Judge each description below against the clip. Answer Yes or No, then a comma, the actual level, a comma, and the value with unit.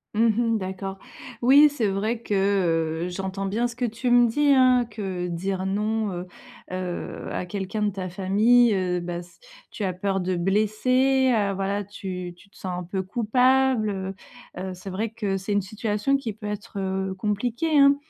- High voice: Yes, high, 205 Hz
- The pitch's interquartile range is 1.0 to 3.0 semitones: No, average, 3.6 semitones